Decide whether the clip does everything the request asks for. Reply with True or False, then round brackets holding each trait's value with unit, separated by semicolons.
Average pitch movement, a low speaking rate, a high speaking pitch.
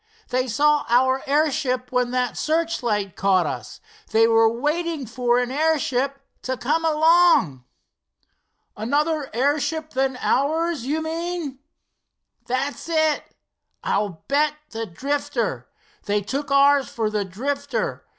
True (4.2 semitones; 120 wpm; 275 Hz)